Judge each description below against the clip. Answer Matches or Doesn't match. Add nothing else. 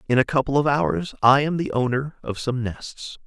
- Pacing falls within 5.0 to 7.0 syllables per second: Doesn't match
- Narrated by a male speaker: Matches